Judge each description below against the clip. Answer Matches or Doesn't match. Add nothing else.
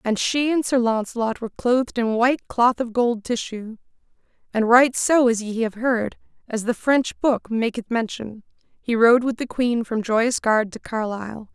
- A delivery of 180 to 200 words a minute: Matches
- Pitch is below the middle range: Doesn't match